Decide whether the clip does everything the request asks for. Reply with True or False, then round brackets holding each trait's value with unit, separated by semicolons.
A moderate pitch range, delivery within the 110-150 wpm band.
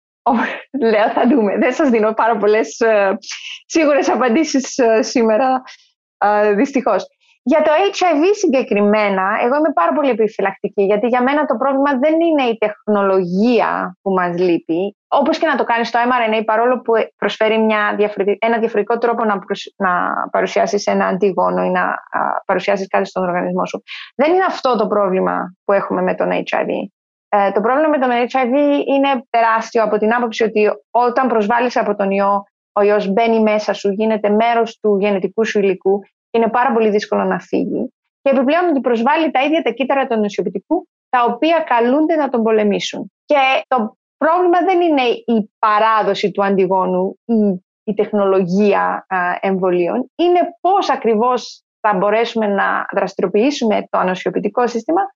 False (4.8 semitones; 160 wpm)